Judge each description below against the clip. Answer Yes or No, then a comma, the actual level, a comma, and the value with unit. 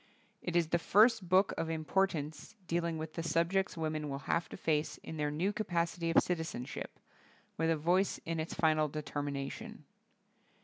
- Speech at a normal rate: Yes, average, 170 wpm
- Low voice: No, medium, 165 Hz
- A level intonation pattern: Yes, narrow, 2.3 semitones